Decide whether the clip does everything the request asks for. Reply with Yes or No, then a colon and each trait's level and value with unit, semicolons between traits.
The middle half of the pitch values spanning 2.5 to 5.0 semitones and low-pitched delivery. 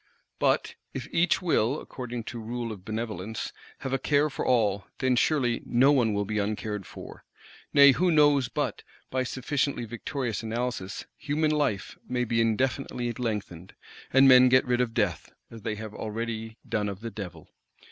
Yes: average, 3.5 semitones; low, 120 Hz